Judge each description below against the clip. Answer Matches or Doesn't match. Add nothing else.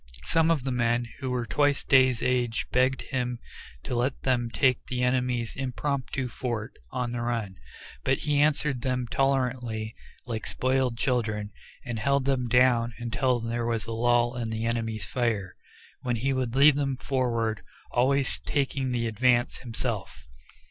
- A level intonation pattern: Matches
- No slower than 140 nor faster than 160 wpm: Matches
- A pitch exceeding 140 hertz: Doesn't match